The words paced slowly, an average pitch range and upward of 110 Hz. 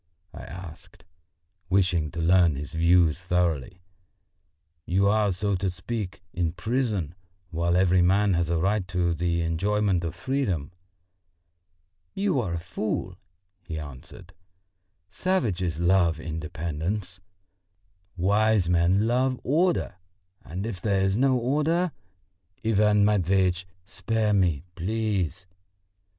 No: slow, 115 wpm; average, 3.7 semitones; very low, 90 Hz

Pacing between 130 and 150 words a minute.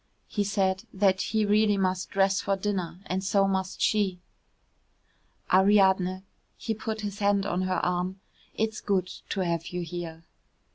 Yes: average, 145 wpm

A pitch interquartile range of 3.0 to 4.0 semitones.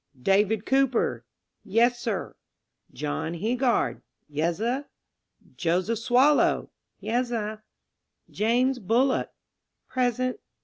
Yes: average, 3.6 semitones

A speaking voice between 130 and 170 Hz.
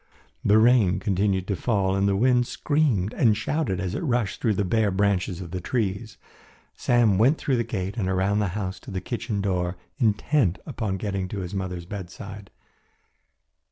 No: low, 100 Hz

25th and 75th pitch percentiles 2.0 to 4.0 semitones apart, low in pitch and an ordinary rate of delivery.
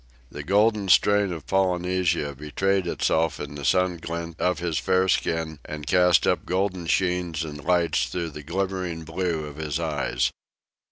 Yes: average, 2.8 semitones; very low, 85 Hz; average, 160 wpm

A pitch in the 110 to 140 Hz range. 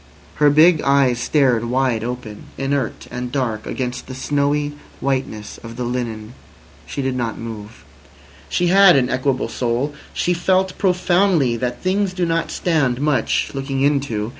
Yes: low, 135 Hz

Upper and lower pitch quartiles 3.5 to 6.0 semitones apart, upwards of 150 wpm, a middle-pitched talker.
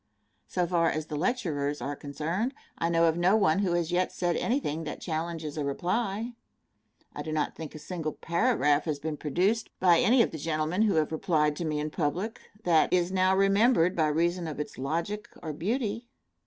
Yes: average, 3.8 semitones; average, 195 wpm; medium, 170 Hz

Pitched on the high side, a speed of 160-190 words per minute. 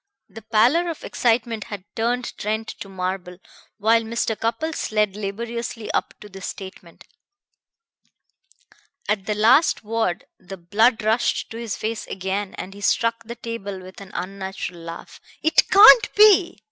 No: high, 220 Hz; average, 145 wpm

